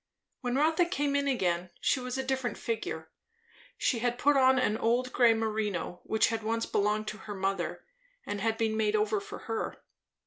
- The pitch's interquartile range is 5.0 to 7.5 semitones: No, average, 3.4 semitones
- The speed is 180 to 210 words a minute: Yes, average, 185 wpm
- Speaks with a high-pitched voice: Yes, high, 225 Hz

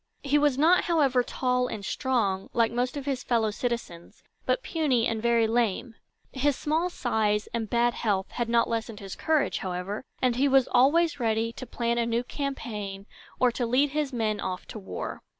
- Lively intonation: No, average, 3.5 semitones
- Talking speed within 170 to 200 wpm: Yes, average, 185 wpm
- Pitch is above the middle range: Yes, high, 240 Hz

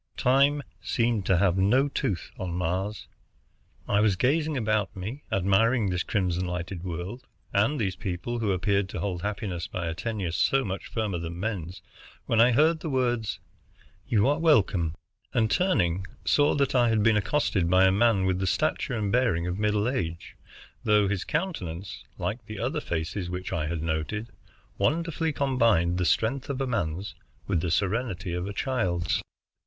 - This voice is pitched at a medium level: No, low, 100 Hz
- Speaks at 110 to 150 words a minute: No, average, 170 wpm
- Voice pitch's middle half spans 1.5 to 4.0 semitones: No, average, 5.3 semitones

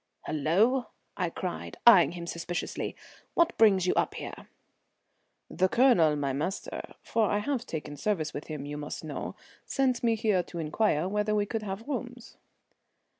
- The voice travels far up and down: Yes, wide, 6.4 semitones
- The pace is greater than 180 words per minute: No, average, 160 wpm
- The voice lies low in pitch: No, high, 190 Hz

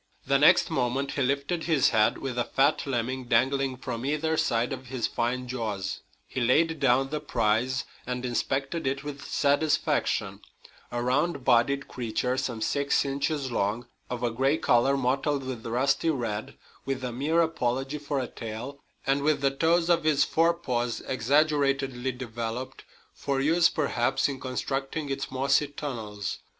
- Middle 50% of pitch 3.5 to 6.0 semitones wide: No, narrow, 2.6 semitones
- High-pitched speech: No, low, 135 Hz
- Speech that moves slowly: No, average, 155 wpm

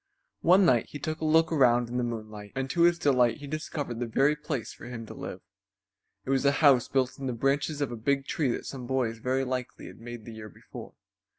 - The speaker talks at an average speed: No, fast, 235 wpm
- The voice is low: Yes, low, 130 Hz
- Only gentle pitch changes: No, average, 3.4 semitones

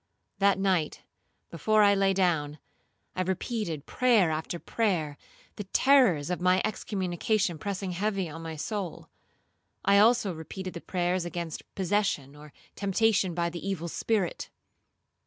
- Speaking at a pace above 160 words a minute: No, slow, 135 wpm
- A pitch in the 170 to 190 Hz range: Yes, medium, 185 Hz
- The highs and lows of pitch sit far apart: No, average, 3.3 semitones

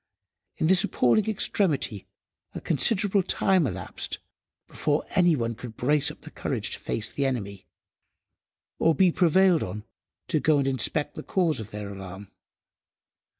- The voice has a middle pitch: Yes, medium, 145 Hz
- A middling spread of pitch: No, wide, 7.7 semitones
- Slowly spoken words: No, average, 145 wpm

